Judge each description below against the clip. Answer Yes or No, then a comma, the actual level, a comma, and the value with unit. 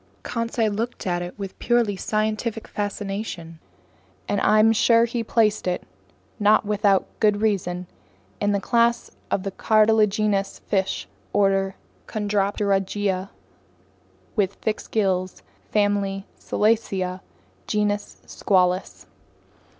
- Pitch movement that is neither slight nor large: No, narrow, 1.9 semitones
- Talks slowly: Yes, slow, 100 wpm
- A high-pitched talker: Yes, high, 205 Hz